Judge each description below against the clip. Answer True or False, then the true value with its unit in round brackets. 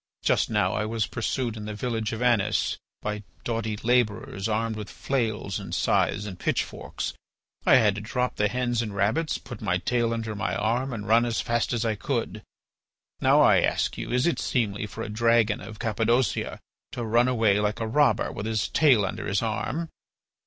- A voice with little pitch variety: True (2.2 semitones)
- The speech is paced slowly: False (190 wpm)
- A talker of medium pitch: False (110 Hz)